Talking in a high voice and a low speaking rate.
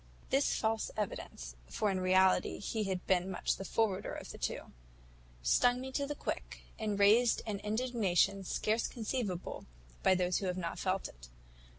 No: high, 200 Hz; average, 170 wpm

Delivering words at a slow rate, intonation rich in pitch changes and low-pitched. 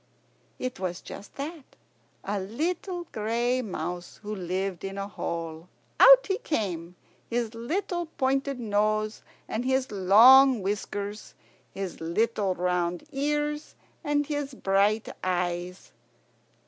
No: slow, 115 wpm; wide, 6.4 semitones; high, 215 Hz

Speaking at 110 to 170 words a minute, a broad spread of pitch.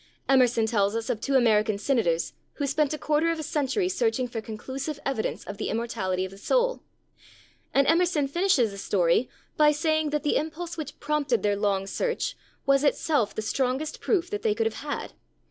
No: average, 190 wpm; wide, 5.8 semitones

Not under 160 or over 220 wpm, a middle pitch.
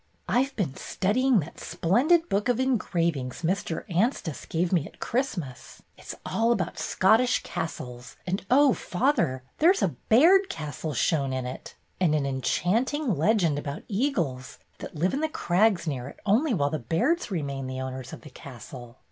Yes: average, 175 wpm; medium, 175 Hz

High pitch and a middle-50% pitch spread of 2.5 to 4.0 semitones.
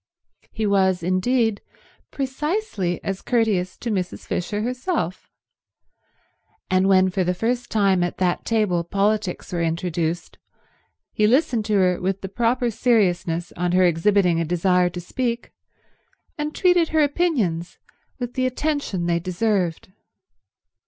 No: high, 195 Hz; average, 5.1 semitones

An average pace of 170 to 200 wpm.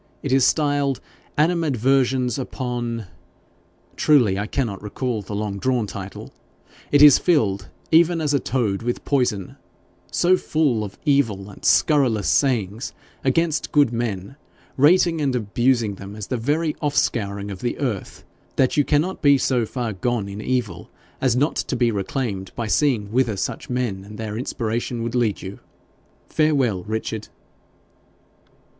No: average, 150 wpm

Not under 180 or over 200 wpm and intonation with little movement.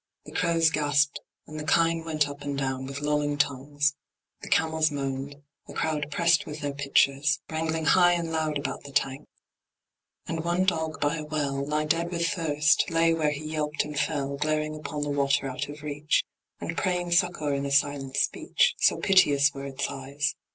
Yes: average, 185 wpm; narrow, 2.1 semitones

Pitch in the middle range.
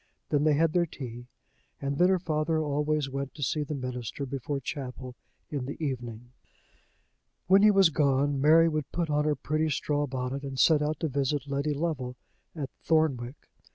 Yes: medium, 145 Hz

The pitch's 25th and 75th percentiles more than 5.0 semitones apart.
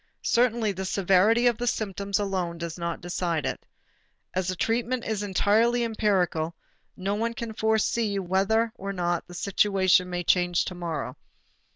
No: average, 3.9 semitones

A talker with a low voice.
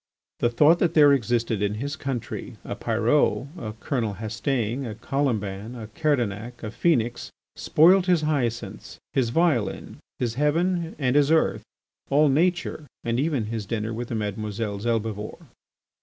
Yes: low, 120 Hz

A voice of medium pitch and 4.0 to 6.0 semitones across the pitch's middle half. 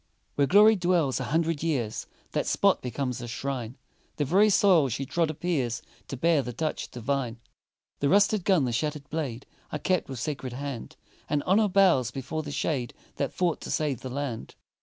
Yes: medium, 145 Hz; average, 4.8 semitones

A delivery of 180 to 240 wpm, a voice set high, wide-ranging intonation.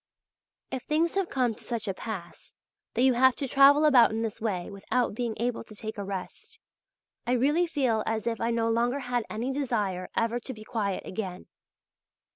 No: average, 195 wpm; high, 235 Hz; average, 3.3 semitones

